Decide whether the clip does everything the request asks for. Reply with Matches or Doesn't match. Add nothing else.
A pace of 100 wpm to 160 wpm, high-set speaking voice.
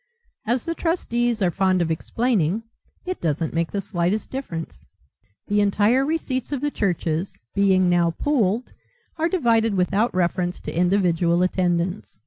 Matches